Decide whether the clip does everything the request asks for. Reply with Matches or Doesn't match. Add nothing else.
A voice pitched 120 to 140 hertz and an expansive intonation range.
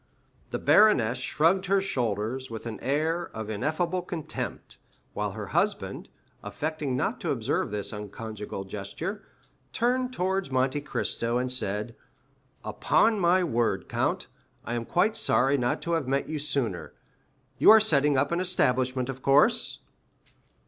Matches